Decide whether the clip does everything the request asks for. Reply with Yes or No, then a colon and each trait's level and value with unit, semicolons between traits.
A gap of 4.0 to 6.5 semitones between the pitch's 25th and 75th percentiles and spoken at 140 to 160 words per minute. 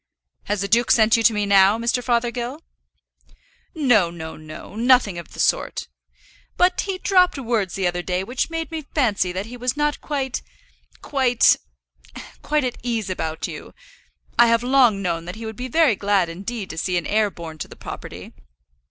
No: average, 5.1 semitones; average, 185 wpm